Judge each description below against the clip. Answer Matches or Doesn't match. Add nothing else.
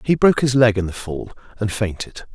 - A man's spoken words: Matches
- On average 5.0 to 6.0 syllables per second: Matches